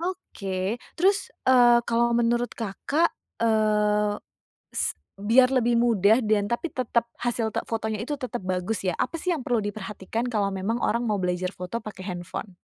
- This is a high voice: Yes, high, 225 Hz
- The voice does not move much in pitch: No, average, 3.1 semitones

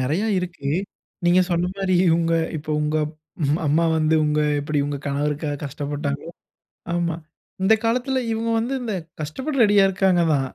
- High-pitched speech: No, medium, 165 Hz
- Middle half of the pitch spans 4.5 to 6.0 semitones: Yes, average, 4.8 semitones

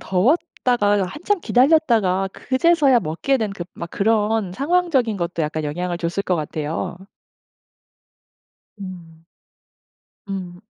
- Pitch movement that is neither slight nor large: No, wide, 6.7 semitones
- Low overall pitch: No, high, 200 Hz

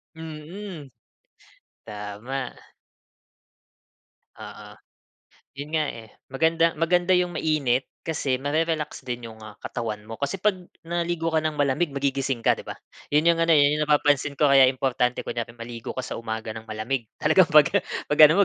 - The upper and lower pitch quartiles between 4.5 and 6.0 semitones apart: Yes, average, 5.1 semitones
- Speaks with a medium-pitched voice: Yes, medium, 145 Hz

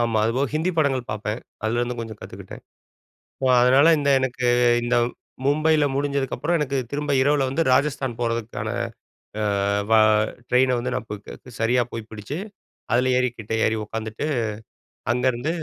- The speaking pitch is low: Yes, low, 125 Hz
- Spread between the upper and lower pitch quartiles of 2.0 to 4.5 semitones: Yes, average, 3.5 semitones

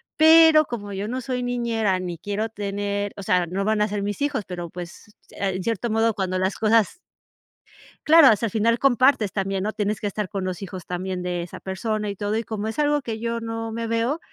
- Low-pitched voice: No, high, 215 Hz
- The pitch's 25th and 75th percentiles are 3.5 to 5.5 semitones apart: No, average, 3.1 semitones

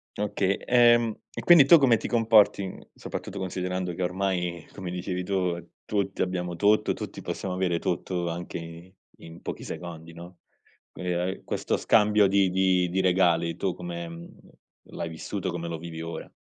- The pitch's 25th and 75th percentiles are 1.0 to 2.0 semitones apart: No, narrow, 2.4 semitones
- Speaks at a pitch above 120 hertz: No, very low, 90 Hz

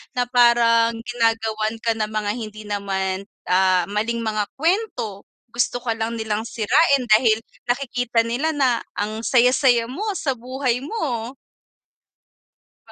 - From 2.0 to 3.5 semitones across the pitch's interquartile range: Yes, narrow, 2.6 semitones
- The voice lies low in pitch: No, high, 230 Hz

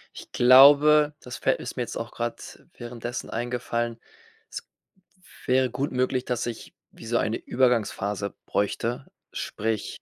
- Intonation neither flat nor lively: No, narrow, 1.8 semitones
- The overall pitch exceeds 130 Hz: No, low, 120 Hz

